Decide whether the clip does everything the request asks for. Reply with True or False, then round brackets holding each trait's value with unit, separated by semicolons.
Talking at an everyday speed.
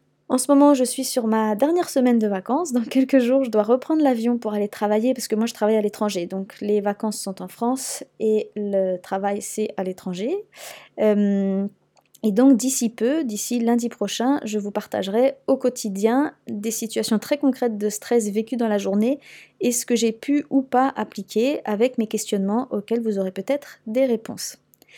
True (190 wpm)